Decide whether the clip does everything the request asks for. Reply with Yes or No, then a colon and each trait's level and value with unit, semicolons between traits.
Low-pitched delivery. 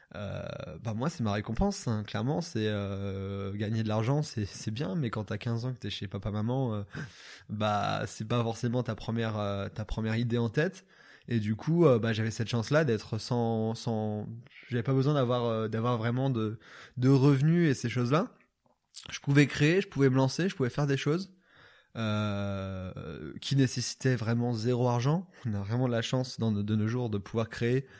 Yes: low, 115 Hz